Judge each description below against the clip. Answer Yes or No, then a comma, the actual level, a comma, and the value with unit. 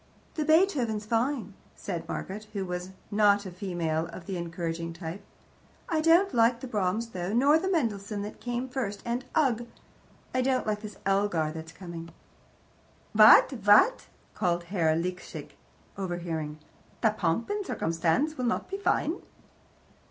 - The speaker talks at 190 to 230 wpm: No, average, 145 wpm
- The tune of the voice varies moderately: No, wide, 6.3 semitones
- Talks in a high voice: Yes, high, 205 Hz